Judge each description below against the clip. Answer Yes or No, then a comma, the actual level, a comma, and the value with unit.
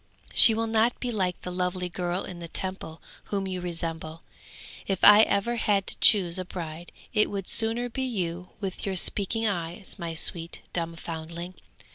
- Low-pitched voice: No, medium, 185 Hz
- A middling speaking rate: Yes, average, 175 wpm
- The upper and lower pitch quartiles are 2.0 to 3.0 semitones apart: No, average, 3.4 semitones